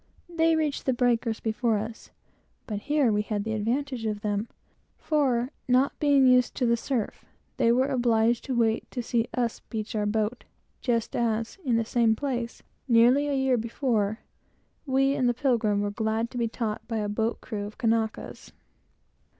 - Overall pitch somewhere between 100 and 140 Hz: No, high, 235 Hz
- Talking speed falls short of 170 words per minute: No, average, 175 wpm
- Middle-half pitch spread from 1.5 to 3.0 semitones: Yes, average, 2.7 semitones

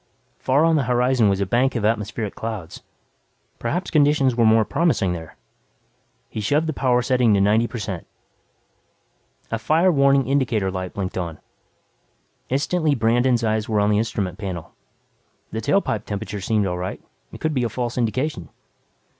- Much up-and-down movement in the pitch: No, average, 4.5 semitones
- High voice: No, low, 115 Hz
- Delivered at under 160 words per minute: No, average, 165 wpm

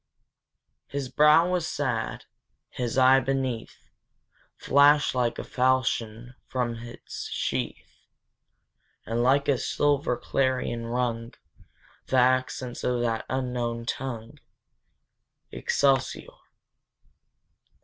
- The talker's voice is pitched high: No, low, 125 Hz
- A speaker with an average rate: No, slow, 90 wpm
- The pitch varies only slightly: Yes, narrow, 2.1 semitones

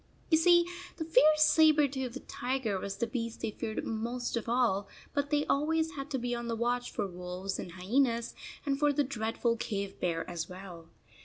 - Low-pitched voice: No, high, 240 Hz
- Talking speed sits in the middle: Yes, average, 190 wpm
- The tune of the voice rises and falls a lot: Yes, wide, 6.0 semitones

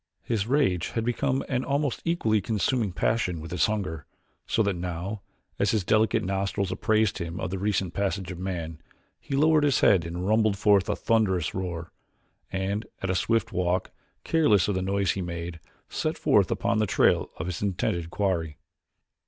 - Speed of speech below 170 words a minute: No, average, 175 wpm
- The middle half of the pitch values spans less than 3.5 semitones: No, average, 3.8 semitones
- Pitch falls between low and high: No, very low, 95 Hz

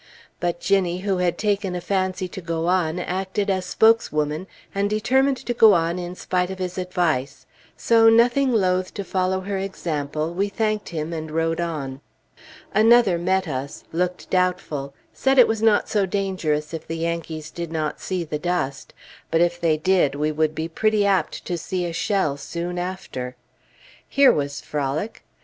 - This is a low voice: No, medium, 180 Hz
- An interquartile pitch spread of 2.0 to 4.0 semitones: Yes, average, 3.6 semitones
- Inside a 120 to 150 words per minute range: No, average, 170 wpm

